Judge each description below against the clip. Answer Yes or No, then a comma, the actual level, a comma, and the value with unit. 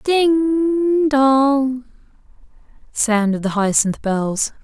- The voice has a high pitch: Yes, very high, 260 Hz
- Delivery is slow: Yes, slow, 80 wpm